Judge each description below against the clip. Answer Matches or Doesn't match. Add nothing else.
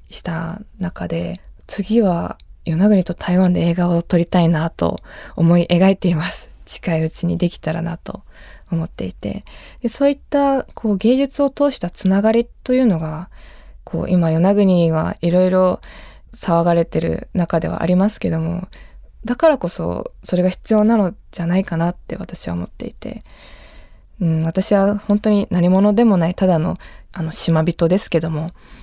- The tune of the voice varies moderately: Matches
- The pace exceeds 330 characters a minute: Doesn't match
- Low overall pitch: Doesn't match